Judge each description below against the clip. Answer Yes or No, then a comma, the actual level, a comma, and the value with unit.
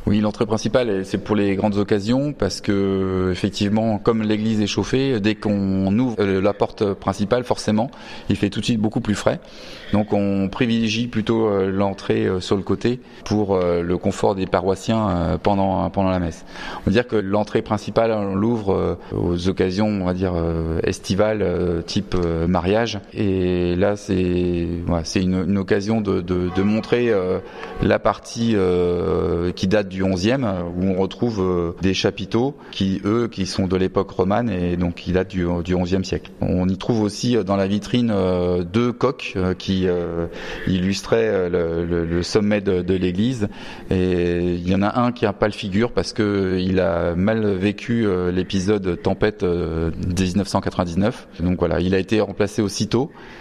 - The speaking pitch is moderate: No, low, 100 Hz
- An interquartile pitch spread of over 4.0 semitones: No, average, 2.8 semitones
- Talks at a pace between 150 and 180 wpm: Yes, average, 170 wpm